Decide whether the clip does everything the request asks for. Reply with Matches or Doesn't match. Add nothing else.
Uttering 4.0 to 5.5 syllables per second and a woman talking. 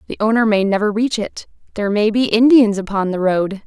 Doesn't match